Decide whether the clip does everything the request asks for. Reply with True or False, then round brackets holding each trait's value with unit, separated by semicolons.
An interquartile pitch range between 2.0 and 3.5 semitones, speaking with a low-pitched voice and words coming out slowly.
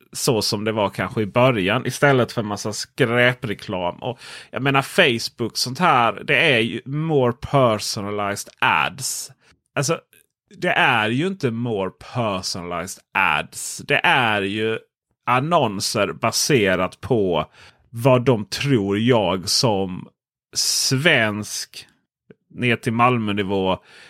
False (4.0 semitones; 115 Hz; 120 wpm)